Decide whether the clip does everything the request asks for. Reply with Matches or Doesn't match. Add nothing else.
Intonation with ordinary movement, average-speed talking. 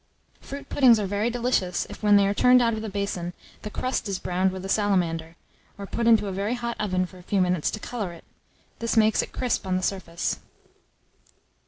Doesn't match